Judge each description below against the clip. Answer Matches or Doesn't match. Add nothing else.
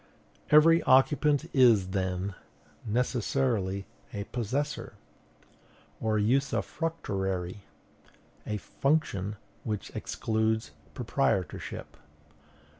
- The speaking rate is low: Matches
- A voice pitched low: Matches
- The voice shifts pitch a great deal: Matches